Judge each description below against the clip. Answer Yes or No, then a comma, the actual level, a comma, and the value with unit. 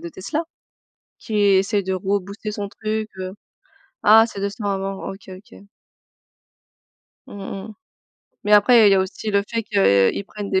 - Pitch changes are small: Yes, narrow, 1.8 semitones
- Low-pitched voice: No, high, 200 Hz